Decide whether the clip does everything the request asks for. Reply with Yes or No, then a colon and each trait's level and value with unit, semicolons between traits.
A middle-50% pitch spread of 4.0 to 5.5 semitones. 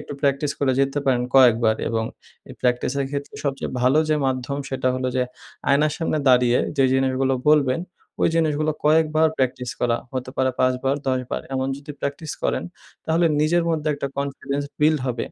No: average, 2.7 semitones